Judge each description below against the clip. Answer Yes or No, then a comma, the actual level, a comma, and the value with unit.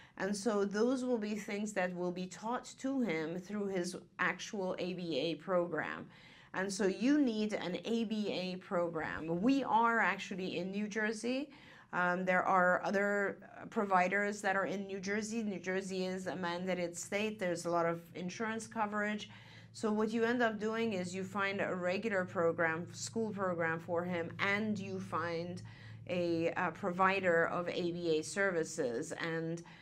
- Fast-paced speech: No, average, 155 wpm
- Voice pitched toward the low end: No, medium, 185 Hz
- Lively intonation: No, average, 3.5 semitones